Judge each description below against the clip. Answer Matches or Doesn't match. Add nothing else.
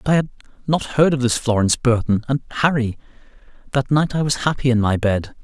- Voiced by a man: Matches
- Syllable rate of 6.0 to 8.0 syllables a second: Matches